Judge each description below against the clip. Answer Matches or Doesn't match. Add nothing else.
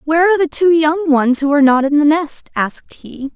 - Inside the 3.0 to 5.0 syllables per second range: Doesn't match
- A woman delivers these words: Matches